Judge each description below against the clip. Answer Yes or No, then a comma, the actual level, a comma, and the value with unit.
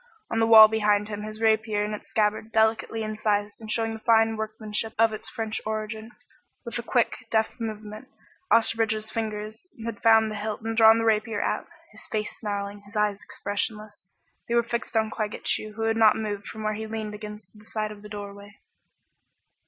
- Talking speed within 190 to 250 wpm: Yes, average, 195 wpm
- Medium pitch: No, high, 215 Hz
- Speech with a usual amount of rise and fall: No, narrow, 1.0 semitones